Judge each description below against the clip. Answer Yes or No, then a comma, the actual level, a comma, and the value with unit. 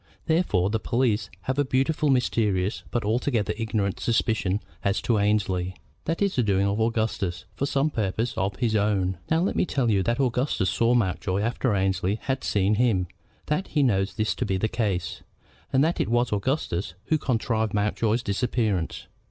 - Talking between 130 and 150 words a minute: No, average, 175 wpm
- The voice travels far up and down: No, average, 4.1 semitones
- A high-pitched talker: No, low, 110 Hz